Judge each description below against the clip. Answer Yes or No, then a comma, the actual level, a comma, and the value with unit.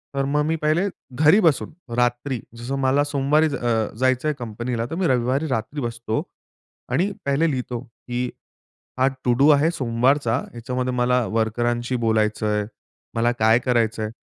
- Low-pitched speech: Yes, low, 125 Hz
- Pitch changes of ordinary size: Yes, average, 3.4 semitones